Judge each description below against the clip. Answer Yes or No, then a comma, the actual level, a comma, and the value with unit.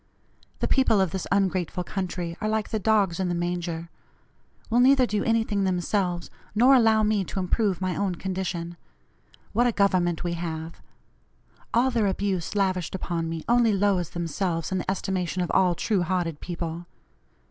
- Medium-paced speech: Yes, average, 165 wpm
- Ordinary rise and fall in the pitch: Yes, average, 3.2 semitones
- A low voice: No, medium, 185 Hz